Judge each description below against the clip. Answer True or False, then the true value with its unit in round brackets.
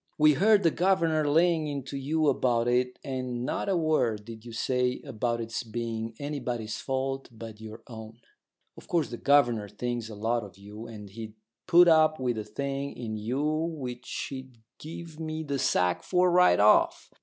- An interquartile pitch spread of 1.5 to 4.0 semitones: False (5.3 semitones)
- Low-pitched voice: True (125 Hz)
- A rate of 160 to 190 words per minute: True (180 wpm)